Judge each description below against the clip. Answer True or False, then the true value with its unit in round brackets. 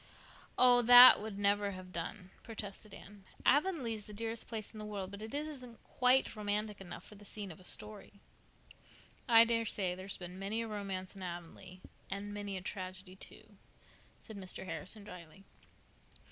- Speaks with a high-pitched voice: True (205 Hz)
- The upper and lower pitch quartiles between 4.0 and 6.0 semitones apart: False (3.0 semitones)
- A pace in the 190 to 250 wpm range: False (165 wpm)